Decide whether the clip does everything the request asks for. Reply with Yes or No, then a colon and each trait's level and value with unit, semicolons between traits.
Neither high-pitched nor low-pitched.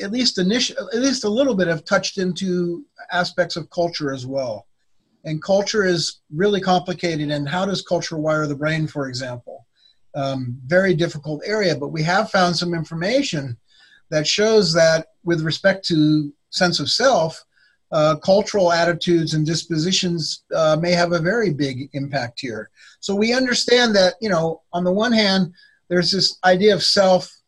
Yes: medium, 175 Hz